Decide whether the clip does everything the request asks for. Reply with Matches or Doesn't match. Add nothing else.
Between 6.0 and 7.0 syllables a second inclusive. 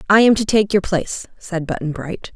Doesn't match